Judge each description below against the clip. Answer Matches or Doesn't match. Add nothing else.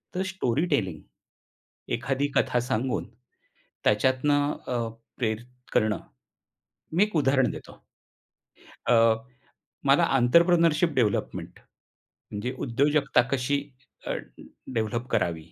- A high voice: Doesn't match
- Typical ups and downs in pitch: Matches